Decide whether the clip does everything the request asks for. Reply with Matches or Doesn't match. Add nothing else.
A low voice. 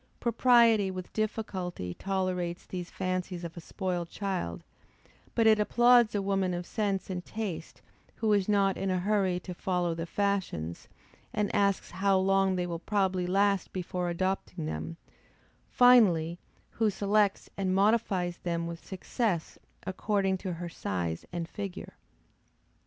Doesn't match